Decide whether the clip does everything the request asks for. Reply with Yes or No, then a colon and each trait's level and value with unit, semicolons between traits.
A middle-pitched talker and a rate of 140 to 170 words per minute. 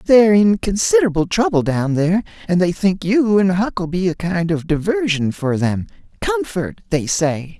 Yes: medium, 180 Hz; average, 165 wpm